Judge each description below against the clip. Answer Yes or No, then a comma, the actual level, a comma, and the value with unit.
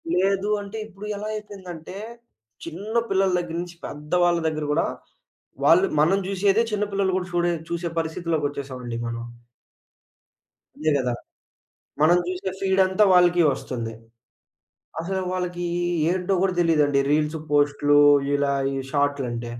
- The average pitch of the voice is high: No, medium, 175 Hz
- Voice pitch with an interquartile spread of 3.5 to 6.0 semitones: Yes, average, 4.5 semitones